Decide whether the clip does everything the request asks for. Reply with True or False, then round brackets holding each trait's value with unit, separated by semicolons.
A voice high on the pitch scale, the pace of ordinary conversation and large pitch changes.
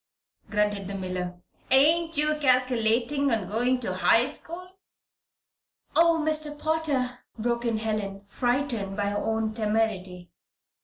False (235 Hz; 120 wpm; 5.9 semitones)